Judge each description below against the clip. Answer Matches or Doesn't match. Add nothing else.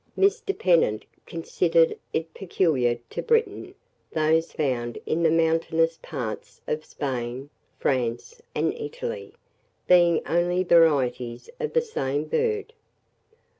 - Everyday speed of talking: Doesn't match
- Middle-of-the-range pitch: Matches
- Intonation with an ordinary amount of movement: Doesn't match